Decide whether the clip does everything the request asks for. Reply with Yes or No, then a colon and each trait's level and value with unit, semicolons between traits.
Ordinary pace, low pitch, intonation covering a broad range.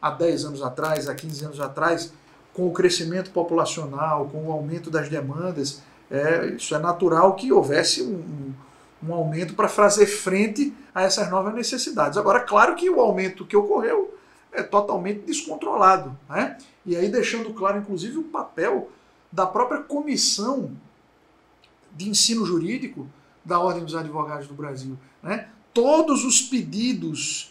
No: average, 150 wpm; medium, 185 Hz; wide, 6.9 semitones